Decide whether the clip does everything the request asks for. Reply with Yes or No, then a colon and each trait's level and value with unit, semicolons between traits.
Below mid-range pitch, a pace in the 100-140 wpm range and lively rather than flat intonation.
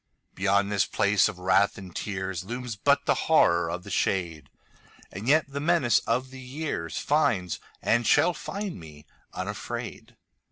Yes: low, 100 Hz; slow, 135 wpm; wide, 6.1 semitones